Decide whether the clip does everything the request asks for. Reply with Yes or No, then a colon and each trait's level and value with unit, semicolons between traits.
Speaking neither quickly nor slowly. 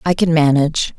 Yes: average, 185 wpm